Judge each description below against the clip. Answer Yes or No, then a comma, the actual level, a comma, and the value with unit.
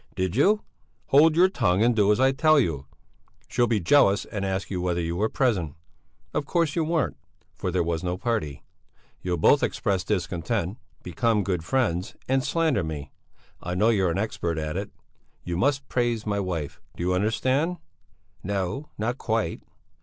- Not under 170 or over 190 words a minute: Yes, average, 175 wpm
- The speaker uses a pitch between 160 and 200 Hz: No, low, 100 Hz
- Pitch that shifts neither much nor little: No, wide, 6.7 semitones